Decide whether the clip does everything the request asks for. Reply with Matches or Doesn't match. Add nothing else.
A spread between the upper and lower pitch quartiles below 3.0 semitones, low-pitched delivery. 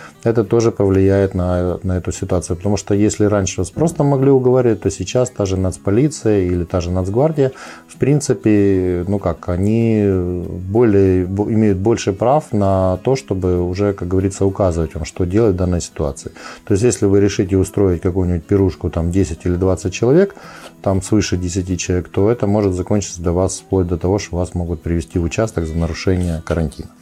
Matches